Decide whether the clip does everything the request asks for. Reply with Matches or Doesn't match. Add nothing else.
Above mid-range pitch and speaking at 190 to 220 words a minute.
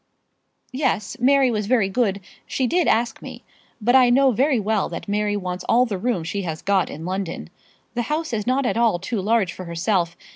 Matches